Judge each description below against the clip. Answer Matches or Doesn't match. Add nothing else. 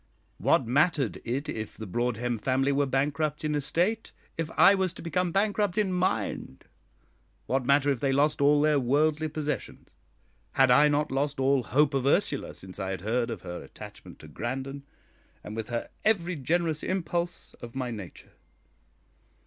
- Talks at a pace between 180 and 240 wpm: Doesn't match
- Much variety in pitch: Doesn't match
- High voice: Doesn't match